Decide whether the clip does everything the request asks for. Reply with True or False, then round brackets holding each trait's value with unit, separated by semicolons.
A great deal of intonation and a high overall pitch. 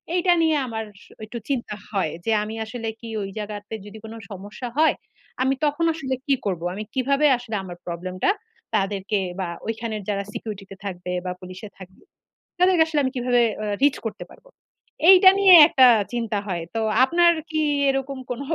True (5.7 semitones; 225 Hz)